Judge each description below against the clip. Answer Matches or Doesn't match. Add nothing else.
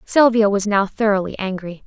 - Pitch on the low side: Doesn't match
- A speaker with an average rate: Matches